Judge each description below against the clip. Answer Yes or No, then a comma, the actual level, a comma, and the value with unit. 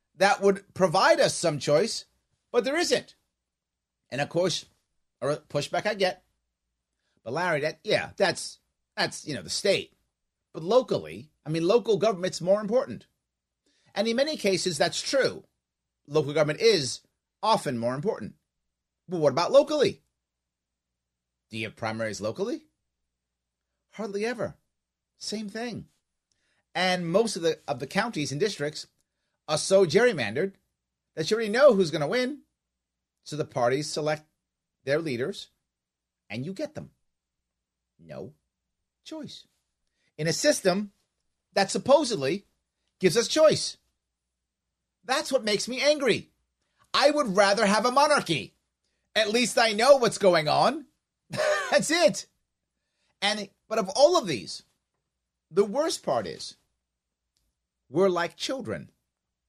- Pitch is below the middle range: No, medium, 170 Hz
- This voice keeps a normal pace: No, slow, 130 wpm